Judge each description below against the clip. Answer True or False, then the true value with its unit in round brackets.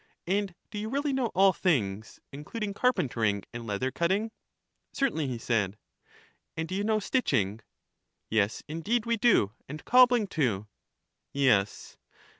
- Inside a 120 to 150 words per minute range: True (140 wpm)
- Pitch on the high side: False (165 Hz)